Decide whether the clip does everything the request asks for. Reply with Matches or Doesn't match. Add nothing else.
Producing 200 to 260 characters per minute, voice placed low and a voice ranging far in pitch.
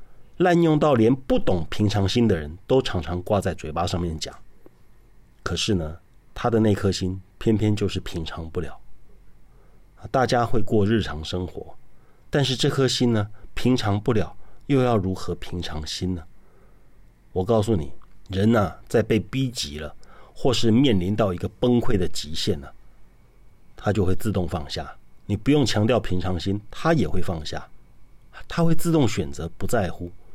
Doesn't match